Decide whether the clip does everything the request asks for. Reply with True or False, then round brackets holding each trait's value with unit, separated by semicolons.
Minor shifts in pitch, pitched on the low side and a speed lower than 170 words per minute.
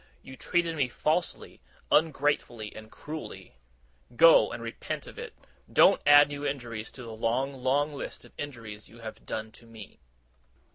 False (4.3 semitones; 130 Hz; 150 wpm)